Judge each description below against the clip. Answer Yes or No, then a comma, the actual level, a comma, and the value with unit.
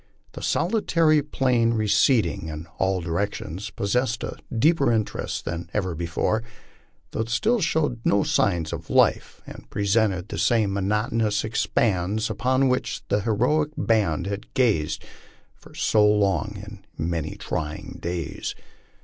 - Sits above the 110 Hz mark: No, low, 105 Hz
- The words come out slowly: Yes, slow, 125 wpm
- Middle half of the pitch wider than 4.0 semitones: Yes, average, 4.6 semitones